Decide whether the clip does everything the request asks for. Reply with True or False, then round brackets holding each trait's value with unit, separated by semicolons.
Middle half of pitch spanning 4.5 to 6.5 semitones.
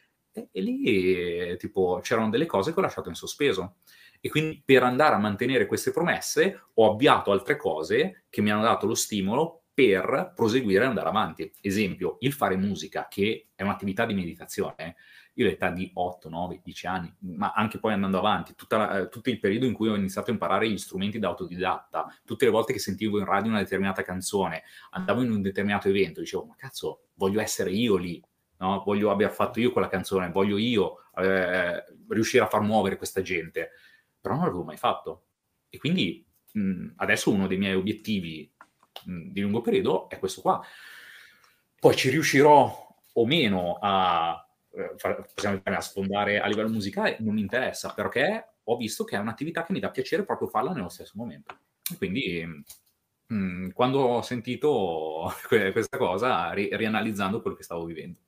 False (3.4 semitones)